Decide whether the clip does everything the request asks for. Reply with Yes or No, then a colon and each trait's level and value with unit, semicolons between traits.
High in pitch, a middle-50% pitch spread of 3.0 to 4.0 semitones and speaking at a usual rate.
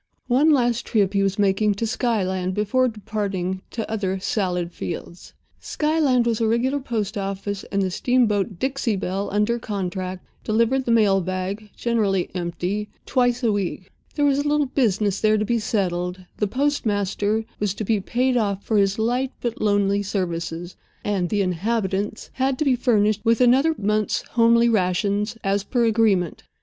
Yes: high, 210 Hz; average, 3.5 semitones; average, 160 wpm